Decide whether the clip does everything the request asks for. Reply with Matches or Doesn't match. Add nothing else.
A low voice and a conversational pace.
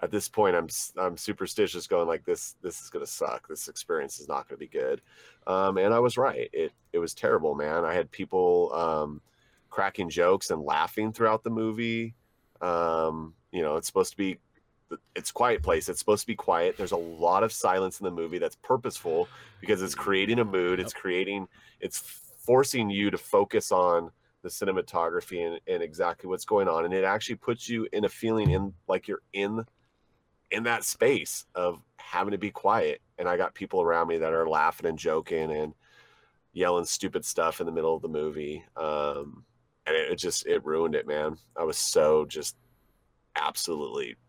Matches